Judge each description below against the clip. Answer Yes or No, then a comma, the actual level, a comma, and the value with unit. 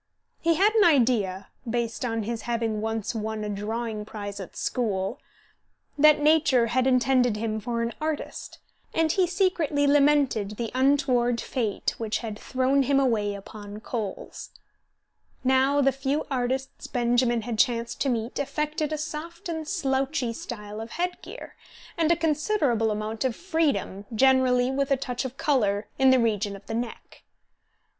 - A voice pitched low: No, very high, 250 Hz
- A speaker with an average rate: Yes, average, 155 wpm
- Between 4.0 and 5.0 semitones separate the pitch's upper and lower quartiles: Yes, average, 4.4 semitones